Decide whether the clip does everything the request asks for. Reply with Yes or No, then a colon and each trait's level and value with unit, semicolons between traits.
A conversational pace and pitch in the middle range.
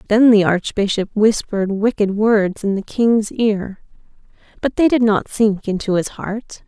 No: average, 160 wpm; high, 210 Hz